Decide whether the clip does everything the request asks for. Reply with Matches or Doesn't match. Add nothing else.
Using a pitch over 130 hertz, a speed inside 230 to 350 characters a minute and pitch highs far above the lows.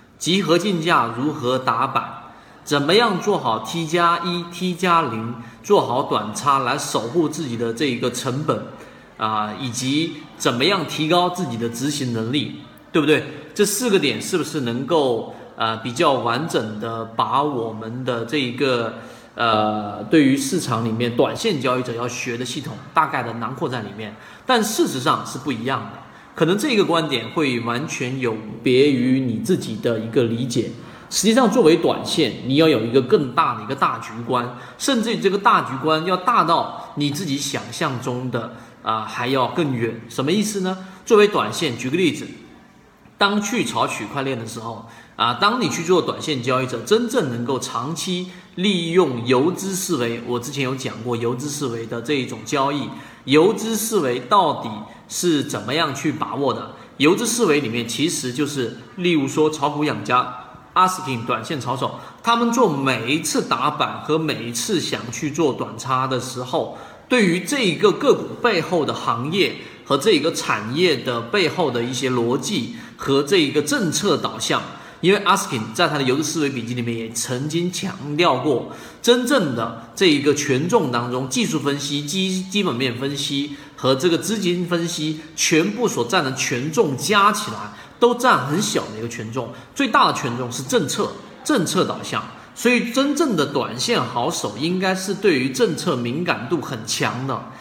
Matches